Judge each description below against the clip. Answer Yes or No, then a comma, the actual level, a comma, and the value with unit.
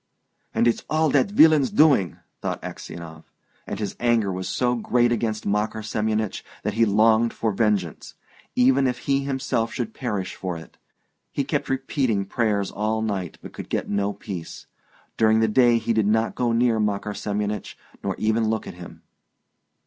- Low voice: Yes, low, 110 Hz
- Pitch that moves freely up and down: No, average, 3.1 semitones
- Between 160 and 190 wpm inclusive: Yes, average, 170 wpm